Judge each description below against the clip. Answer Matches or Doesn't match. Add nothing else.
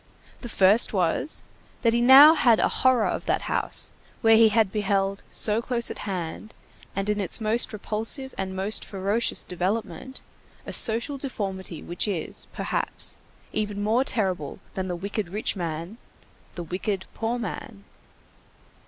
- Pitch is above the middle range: Matches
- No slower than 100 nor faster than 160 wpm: Matches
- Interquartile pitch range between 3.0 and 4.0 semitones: Matches